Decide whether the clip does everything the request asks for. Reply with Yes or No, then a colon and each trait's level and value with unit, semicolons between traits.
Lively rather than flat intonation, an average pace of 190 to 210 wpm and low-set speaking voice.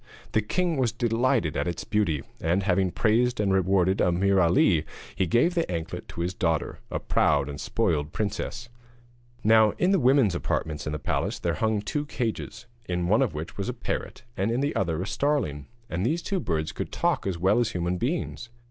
Yes: wide, 5.7 semitones; average, 200 wpm; low, 100 Hz